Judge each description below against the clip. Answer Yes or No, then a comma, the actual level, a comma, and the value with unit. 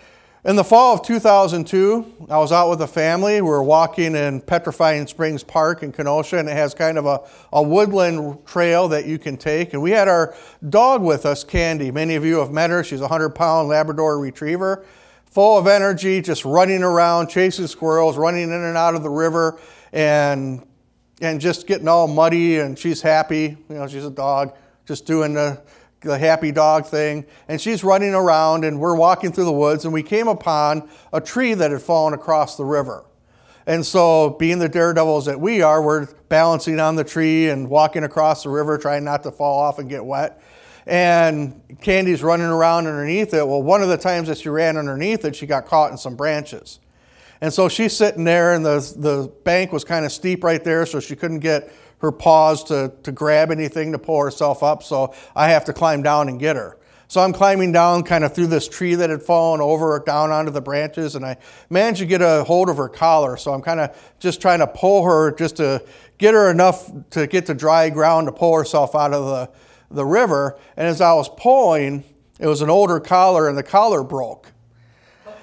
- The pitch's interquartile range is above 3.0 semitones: No, narrow, 2.6 semitones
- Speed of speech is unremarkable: No, fast, 210 wpm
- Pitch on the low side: No, medium, 160 Hz